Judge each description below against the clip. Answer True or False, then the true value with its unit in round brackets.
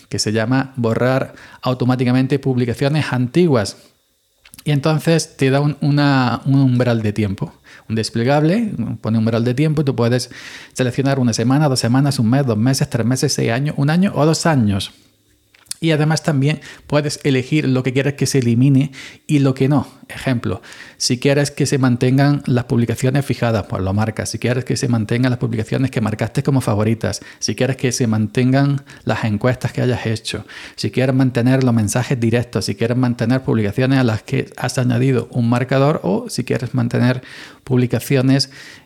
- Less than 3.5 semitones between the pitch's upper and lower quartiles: True (3.0 semitones)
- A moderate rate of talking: True (180 wpm)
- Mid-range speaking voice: False (130 Hz)